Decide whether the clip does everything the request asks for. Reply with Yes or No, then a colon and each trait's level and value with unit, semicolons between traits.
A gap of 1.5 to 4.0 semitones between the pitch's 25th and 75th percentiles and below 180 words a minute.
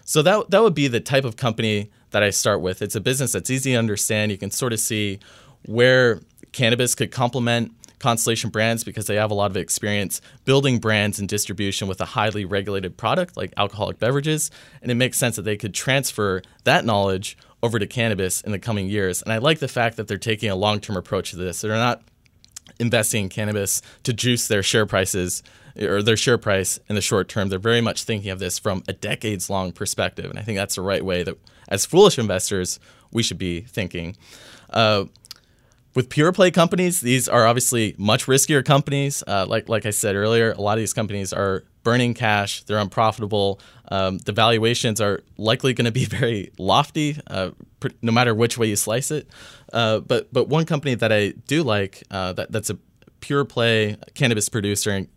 No: average, 3.3 semitones; fast, 205 wpm